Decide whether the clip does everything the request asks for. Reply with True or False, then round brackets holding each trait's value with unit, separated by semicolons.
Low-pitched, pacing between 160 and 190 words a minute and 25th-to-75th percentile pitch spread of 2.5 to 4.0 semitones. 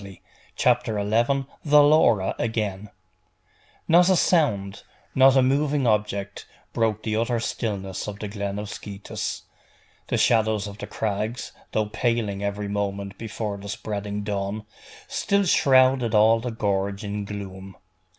False (105 Hz; 135 wpm; 2.8 semitones)